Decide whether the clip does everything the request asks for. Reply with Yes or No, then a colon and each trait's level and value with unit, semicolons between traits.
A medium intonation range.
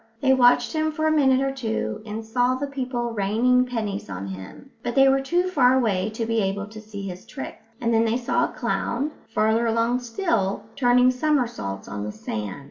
Yes: average, 4.1 semitones